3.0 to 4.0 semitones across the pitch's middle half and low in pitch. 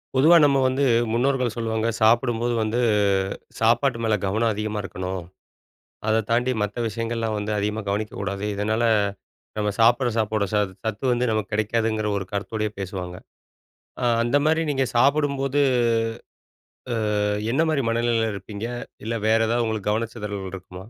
No: narrow, 2.4 semitones; low, 110 Hz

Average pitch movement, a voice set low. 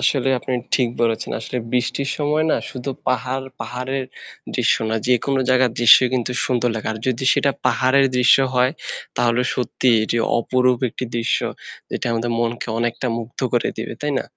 No: narrow, 1.8 semitones; low, 125 Hz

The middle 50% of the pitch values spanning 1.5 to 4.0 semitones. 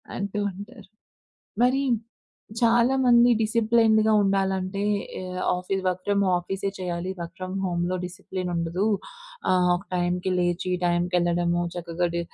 Yes: average, 2.7 semitones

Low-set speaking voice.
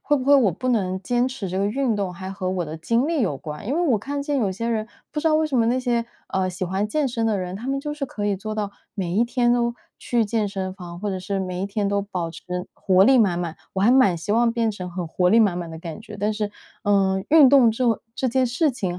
No: high, 210 Hz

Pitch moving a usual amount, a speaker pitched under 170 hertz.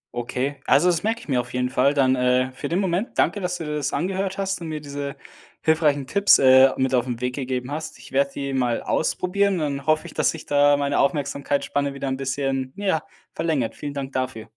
Yes: average, 3.4 semitones; medium, 140 Hz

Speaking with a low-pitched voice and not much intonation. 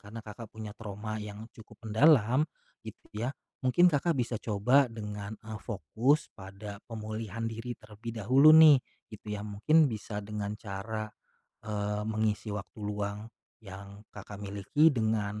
Yes: low, 110 Hz; narrow, 2.0 semitones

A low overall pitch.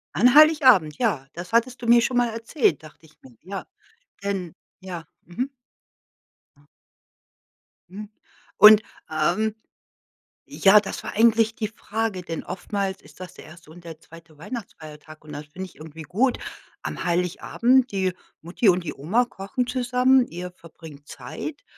No: high, 190 Hz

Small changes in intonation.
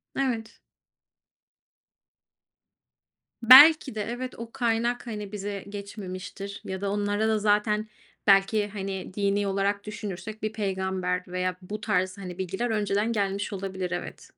Yes: narrow, 2.1 semitones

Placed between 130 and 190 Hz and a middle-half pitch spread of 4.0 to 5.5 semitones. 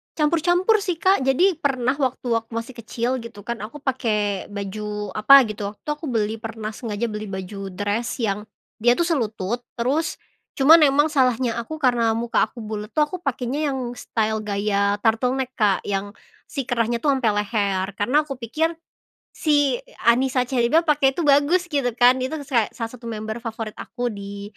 No: high, 235 Hz; average, 4.5 semitones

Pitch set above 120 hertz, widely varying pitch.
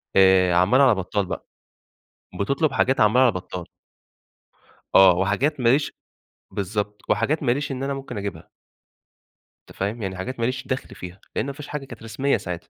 No: low, 110 Hz; wide, 6.0 semitones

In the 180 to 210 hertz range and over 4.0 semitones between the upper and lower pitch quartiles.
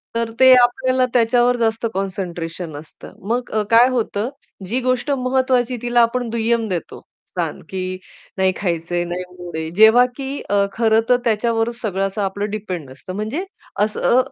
No: high, 220 Hz; average, 4.5 semitones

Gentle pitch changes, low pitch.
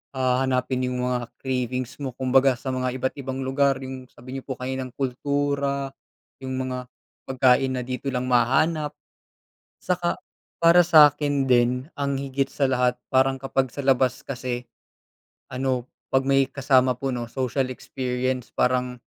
Yes: narrow, 1.3 semitones; low, 130 Hz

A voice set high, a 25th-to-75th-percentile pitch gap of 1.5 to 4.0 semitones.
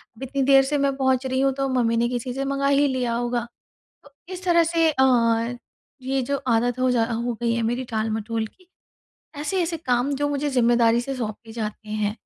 Yes: very high, 255 Hz; average, 3.0 semitones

